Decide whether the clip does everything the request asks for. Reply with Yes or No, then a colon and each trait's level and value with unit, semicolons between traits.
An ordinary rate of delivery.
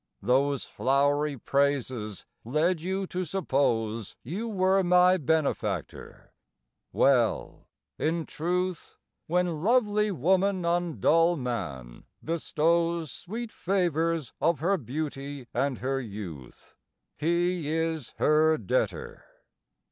No: slow, 100 wpm